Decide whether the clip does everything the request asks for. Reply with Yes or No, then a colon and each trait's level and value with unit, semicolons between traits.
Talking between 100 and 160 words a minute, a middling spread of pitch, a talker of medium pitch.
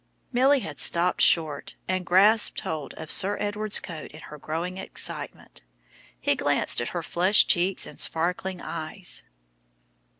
Yes: average, 140 wpm; average, 3.8 semitones; medium, 180 Hz